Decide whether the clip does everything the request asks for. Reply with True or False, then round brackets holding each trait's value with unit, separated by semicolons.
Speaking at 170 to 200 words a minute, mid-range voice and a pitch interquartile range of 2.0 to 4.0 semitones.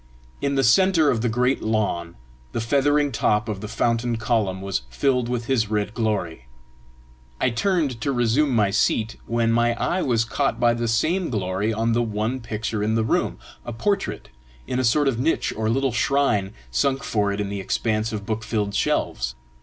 False (190 wpm; 115 Hz; 3.4 semitones)